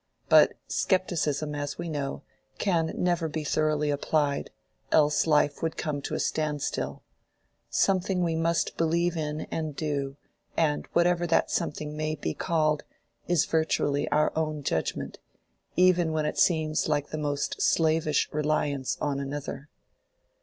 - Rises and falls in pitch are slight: Yes, narrow, 1.9 semitones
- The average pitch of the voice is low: No, medium, 155 Hz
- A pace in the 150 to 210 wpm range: No, average, 140 wpm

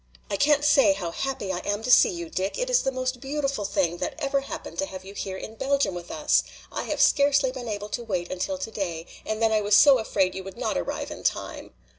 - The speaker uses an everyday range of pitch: No, wide, 6.1 semitones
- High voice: Yes, high, 220 Hz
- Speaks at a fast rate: Yes, fast, 245 wpm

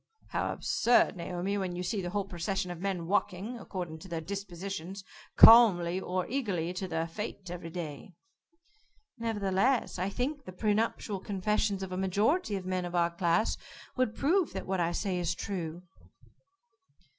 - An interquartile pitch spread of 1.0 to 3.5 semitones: Yes, average, 2.9 semitones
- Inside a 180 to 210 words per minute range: No, average, 165 wpm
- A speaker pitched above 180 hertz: Yes, high, 190 Hz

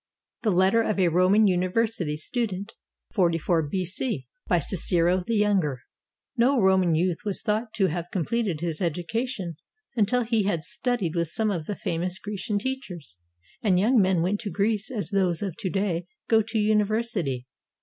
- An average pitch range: Yes, average, 4.1 semitones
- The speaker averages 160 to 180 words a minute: Yes, average, 170 wpm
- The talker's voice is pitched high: Yes, high, 195 Hz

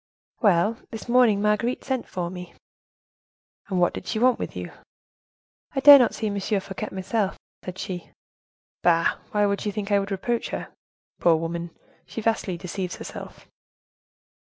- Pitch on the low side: No, high, 200 Hz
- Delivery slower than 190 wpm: Yes, average, 160 wpm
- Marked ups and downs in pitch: No, average, 3.6 semitones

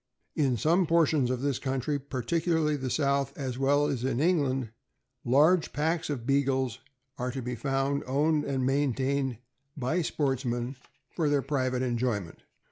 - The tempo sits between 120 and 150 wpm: Yes, average, 145 wpm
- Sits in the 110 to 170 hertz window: Yes, low, 135 Hz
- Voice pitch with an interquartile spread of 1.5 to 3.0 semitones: Yes, narrow, 2.4 semitones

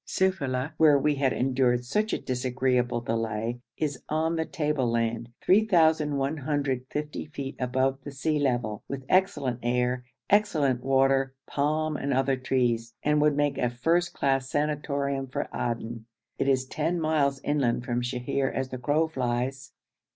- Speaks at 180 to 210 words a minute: No, average, 145 wpm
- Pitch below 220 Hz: Yes, low, 135 Hz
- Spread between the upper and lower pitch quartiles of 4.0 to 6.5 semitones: No, average, 3.2 semitones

